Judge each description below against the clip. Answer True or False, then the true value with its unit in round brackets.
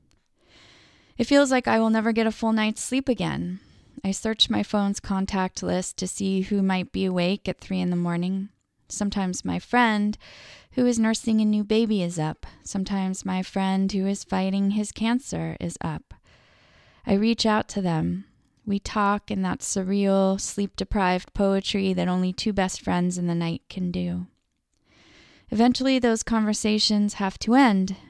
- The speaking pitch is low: False (195 Hz)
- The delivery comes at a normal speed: True (170 wpm)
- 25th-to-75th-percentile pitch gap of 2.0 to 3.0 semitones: True (2.7 semitones)